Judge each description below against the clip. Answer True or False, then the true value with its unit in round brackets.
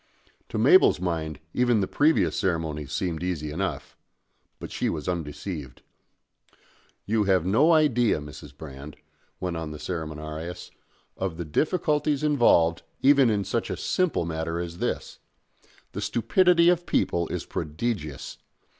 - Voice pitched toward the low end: True (90 Hz)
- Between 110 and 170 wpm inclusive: True (135 wpm)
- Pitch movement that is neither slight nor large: False (7.4 semitones)